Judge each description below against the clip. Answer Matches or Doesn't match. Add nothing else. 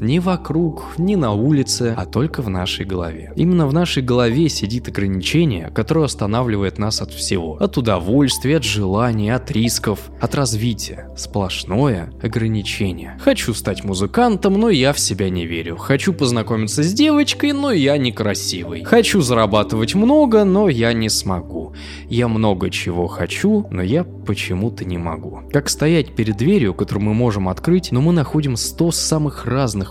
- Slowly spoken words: Doesn't match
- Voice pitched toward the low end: Matches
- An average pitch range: Doesn't match